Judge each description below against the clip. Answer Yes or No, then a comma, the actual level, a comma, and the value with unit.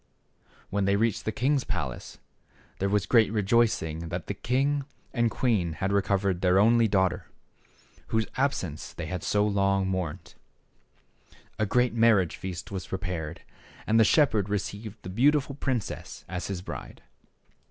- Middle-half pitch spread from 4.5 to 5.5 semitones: No, average, 3.9 semitones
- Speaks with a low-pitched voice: Yes, low, 100 Hz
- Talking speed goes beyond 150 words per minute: No, average, 145 wpm